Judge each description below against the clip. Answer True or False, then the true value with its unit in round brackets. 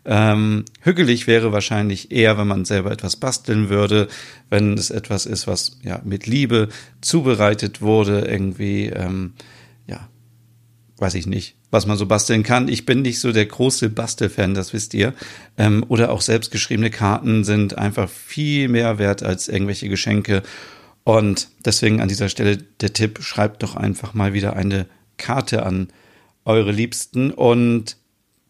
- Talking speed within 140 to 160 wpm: True (150 wpm)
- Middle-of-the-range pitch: False (110 Hz)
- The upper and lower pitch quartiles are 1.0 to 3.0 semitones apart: True (2.5 semitones)